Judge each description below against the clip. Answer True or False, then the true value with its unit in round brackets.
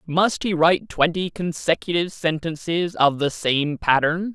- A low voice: False (160 Hz)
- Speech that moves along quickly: False (140 wpm)